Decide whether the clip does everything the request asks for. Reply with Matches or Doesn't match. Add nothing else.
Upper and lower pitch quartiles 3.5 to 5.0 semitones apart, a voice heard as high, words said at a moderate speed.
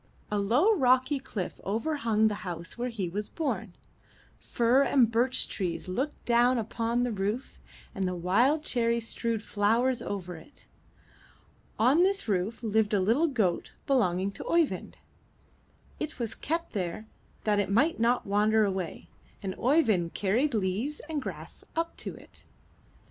Matches